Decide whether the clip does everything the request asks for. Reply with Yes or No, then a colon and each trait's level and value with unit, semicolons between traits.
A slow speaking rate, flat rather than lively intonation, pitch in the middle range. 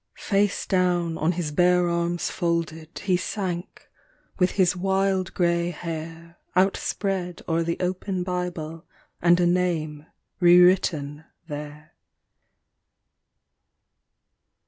Yes: slow, 100 wpm; narrow, 1.7 semitones; medium, 175 Hz